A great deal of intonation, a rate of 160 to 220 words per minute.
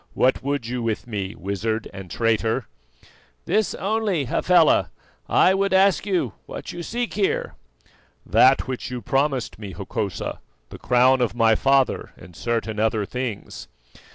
No: wide, 7.6 semitones; average, 145 wpm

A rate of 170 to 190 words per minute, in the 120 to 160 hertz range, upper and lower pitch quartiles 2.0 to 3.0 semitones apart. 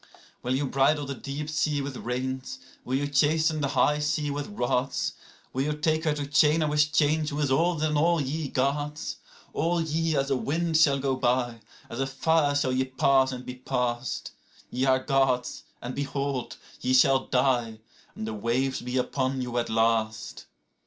Yes: average, 180 wpm; low, 135 Hz; average, 2.7 semitones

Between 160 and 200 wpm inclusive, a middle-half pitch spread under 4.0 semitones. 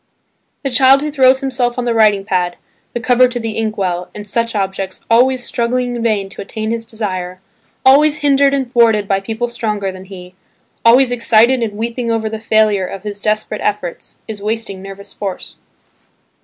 Yes: average, 185 wpm; average, 3.5 semitones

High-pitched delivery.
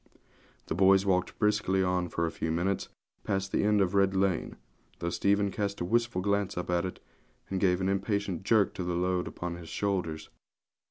No: very low, 95 Hz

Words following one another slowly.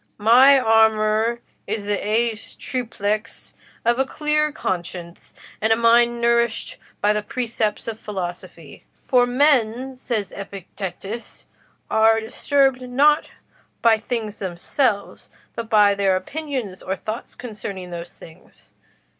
Yes: slow, 120 wpm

